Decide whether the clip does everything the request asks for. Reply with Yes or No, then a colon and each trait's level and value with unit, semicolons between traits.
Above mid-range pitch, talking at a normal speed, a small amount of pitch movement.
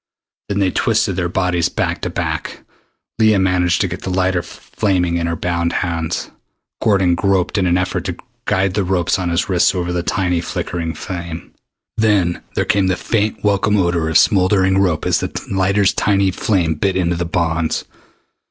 No: very low, 90 Hz; average, 180 wpm; narrow, 2.1 semitones